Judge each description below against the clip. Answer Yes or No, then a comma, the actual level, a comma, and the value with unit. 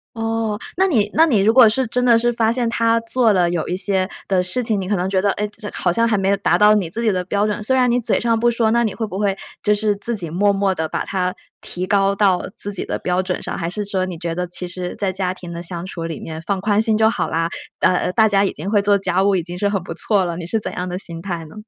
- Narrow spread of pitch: No, average, 3.4 semitones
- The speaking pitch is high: Yes, high, 200 Hz